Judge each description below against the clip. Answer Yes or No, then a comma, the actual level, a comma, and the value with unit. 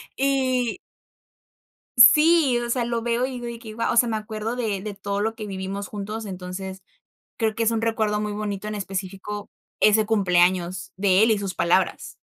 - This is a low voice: No, high, 215 Hz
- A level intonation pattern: No, average, 3.0 semitones